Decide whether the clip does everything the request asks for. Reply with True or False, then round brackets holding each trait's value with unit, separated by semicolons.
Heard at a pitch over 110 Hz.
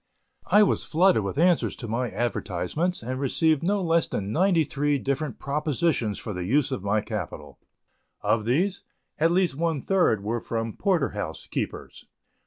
True (140 Hz)